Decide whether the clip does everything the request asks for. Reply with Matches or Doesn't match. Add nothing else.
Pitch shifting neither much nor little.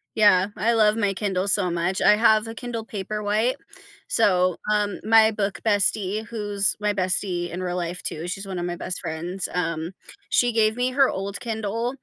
Matches